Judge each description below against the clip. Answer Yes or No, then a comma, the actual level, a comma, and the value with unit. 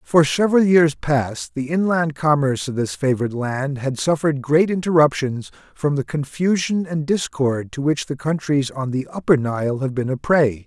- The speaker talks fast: No, average, 180 wpm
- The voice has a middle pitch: Yes, medium, 145 Hz